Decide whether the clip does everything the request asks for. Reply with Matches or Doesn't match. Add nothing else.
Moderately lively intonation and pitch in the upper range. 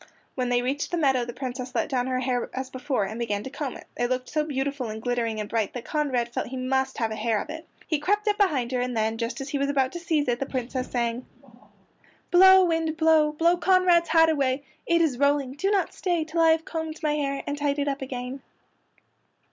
Matches